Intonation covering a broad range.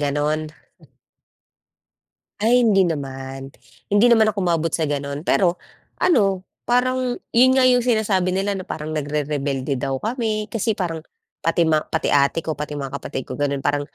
Yes: wide, 7.0 semitones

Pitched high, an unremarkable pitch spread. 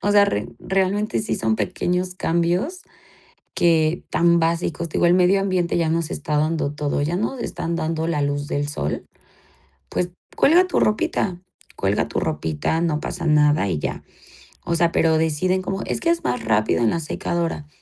No: medium, 170 Hz; average, 3.6 semitones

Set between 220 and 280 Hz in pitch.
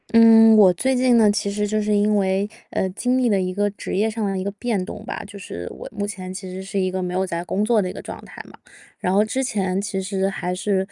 No: high, 200 Hz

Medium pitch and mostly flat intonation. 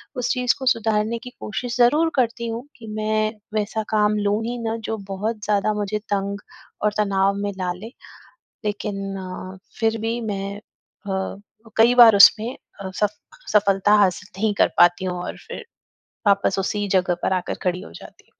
No: high, 210 Hz; narrow, 2.3 semitones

